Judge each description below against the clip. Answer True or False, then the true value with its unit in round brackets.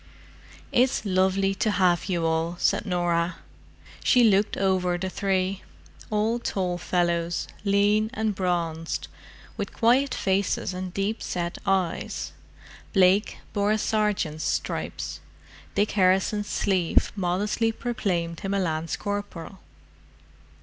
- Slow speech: True (115 wpm)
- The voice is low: False (190 Hz)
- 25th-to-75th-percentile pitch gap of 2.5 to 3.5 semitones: True (2.8 semitones)